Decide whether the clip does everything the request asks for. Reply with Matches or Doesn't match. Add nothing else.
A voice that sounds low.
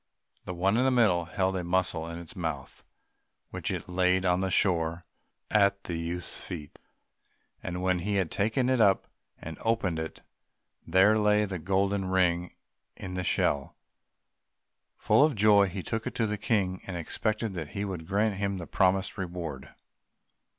Matches